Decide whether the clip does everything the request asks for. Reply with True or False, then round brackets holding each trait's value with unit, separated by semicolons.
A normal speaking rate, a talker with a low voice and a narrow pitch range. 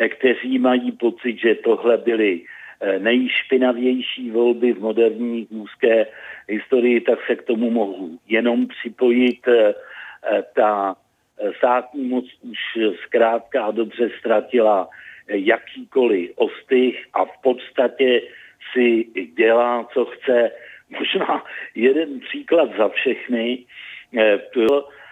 False (100 wpm; 120 Hz; 1.9 semitones)